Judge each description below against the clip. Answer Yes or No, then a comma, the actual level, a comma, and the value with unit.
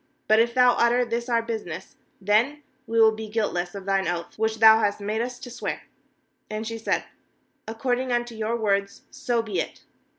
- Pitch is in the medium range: No, high, 225 Hz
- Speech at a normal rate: Yes, average, 190 wpm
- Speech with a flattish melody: Yes, narrow, 2.3 semitones